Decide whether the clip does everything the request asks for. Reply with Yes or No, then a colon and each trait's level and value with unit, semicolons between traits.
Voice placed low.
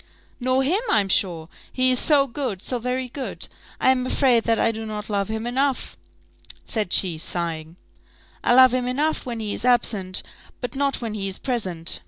No: high, 235 Hz